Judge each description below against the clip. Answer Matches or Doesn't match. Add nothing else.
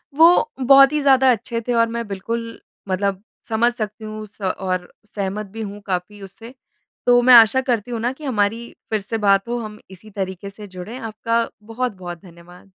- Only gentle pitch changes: Doesn't match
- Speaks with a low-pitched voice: Doesn't match